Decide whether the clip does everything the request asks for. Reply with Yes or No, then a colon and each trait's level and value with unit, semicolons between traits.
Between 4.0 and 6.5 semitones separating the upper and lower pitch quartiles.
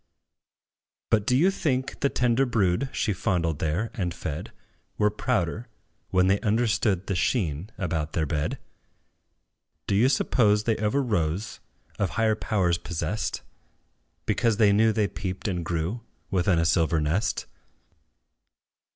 Yes: average, 4.7 semitones